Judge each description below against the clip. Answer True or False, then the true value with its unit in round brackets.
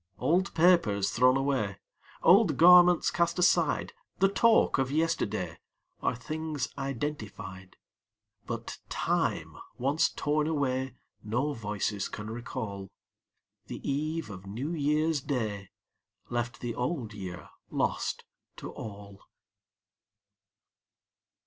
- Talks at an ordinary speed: False (105 wpm)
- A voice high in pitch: False (135 Hz)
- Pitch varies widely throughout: True (6.9 semitones)